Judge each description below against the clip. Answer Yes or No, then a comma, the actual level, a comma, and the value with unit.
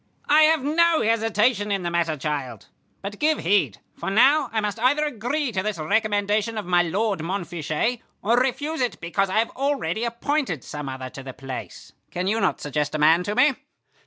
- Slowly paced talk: No, average, 190 wpm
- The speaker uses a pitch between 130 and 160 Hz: No, high, 210 Hz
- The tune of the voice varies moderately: No, wide, 6.8 semitones